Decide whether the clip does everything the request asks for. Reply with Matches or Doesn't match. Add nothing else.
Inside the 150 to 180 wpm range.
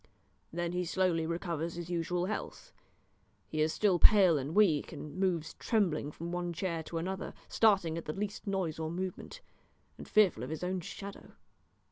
Matches